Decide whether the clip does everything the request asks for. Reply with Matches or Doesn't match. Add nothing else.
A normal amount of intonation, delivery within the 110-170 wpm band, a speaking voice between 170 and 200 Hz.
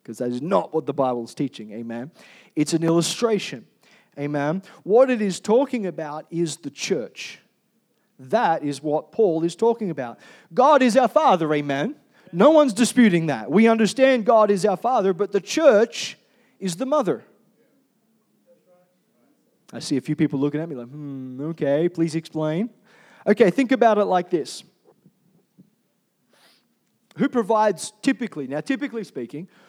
Doesn't match